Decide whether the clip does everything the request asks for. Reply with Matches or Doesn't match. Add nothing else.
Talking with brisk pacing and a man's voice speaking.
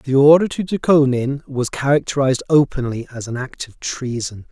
Doesn't match